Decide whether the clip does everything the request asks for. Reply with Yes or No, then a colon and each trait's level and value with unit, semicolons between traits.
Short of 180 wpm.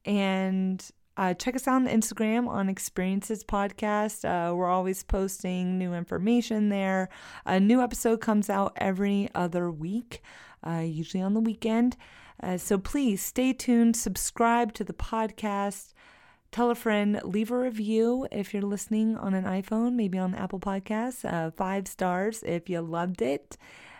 Yes: average, 155 wpm